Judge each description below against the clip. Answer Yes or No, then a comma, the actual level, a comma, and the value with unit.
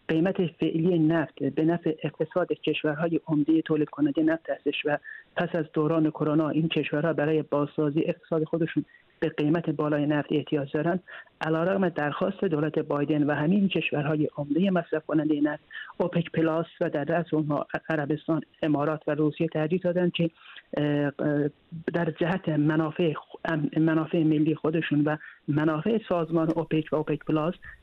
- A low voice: No, medium, 155 Hz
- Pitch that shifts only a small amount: Yes, narrow, 1.8 semitones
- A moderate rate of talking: Yes, average, 140 wpm